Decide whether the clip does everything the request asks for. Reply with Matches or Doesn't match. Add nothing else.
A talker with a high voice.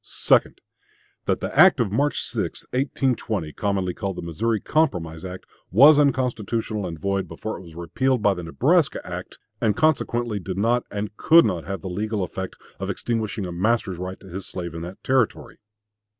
Doesn't match